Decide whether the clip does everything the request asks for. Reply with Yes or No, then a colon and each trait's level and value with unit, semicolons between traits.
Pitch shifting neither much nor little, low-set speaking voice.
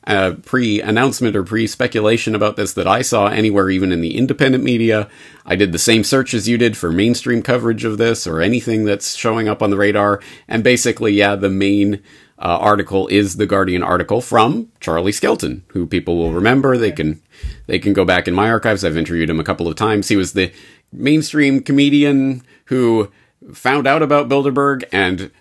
Yes: average, 4.1 semitones; low, 105 Hz